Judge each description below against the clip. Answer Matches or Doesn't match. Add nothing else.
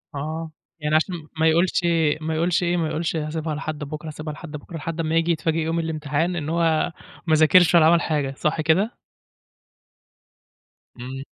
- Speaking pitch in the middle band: Matches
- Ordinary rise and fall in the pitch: Doesn't match